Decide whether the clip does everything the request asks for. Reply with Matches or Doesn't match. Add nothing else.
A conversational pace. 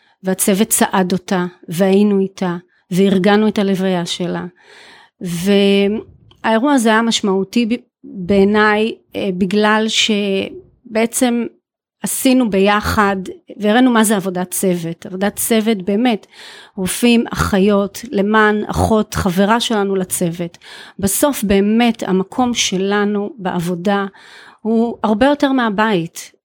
Doesn't match